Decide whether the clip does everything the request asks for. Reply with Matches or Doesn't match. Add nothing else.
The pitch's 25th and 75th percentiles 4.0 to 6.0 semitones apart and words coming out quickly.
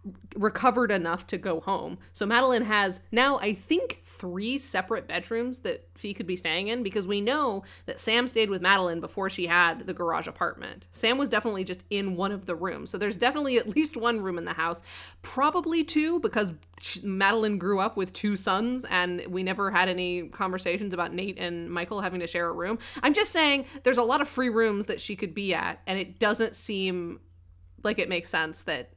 Matches